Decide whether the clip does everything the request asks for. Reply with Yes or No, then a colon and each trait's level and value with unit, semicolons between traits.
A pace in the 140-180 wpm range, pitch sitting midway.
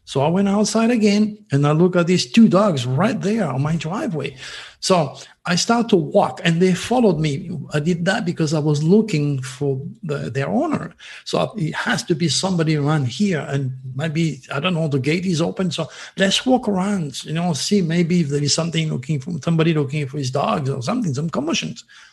No: fast, 205 wpm; medium, 165 Hz